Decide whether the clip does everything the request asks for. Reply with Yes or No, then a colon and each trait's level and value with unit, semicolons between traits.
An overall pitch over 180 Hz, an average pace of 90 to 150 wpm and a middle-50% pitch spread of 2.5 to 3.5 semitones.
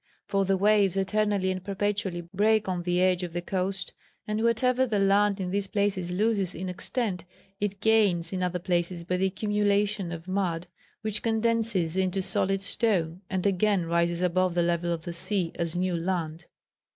No: high, 190 Hz; average, 175 wpm; average, 2.8 semitones